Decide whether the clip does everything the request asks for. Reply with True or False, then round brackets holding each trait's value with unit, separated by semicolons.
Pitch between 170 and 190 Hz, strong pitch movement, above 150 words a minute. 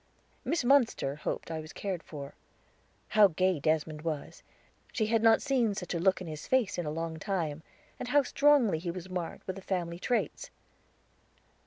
True (185 Hz; 5.7 semitones; 185 wpm)